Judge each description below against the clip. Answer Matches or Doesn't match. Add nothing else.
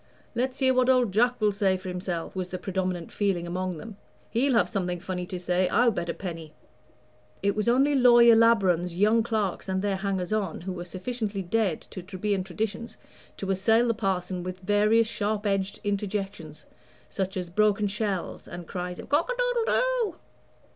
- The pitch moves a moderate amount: Matches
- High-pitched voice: Matches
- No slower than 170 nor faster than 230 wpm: Matches